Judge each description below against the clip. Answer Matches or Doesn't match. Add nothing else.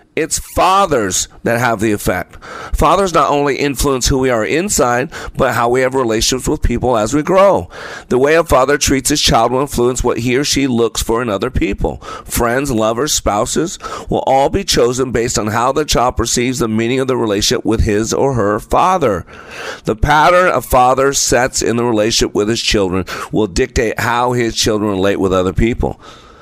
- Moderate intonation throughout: Matches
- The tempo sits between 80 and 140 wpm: Doesn't match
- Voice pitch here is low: Matches